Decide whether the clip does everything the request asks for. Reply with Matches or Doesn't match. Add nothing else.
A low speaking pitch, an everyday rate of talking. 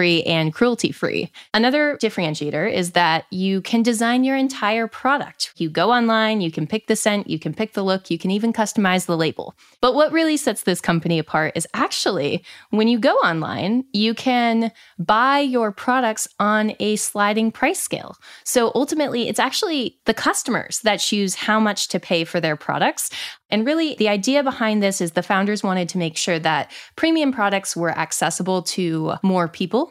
Doesn't match